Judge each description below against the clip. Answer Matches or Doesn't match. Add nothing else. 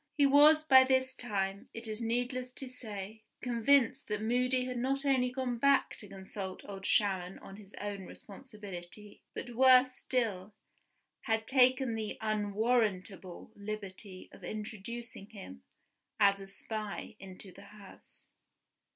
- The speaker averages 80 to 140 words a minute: Matches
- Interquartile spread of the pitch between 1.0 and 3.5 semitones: Doesn't match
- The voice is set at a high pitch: Matches